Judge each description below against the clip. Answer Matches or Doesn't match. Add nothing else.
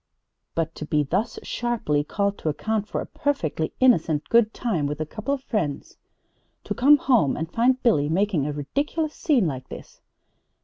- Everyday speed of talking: Matches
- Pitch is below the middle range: Doesn't match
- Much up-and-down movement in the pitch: Matches